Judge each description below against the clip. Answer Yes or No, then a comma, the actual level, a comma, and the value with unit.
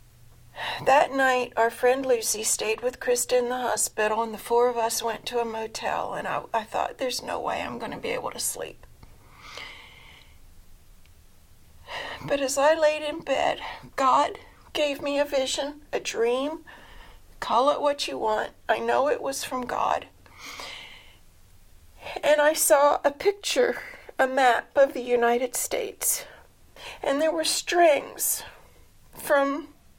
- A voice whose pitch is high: Yes, very high, 255 Hz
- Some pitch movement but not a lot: Yes, average, 4.6 semitones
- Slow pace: No, average, 150 wpm